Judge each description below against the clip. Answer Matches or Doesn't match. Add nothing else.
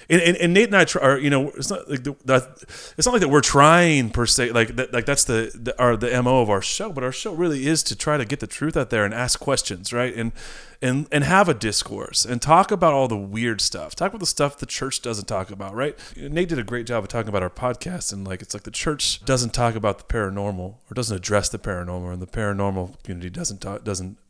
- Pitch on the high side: Doesn't match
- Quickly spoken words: Matches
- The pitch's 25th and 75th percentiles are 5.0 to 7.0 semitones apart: Matches